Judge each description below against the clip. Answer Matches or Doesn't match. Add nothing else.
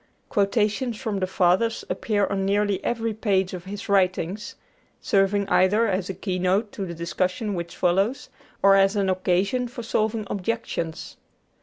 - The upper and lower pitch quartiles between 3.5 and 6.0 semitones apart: Doesn't match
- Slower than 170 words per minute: Matches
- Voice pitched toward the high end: Matches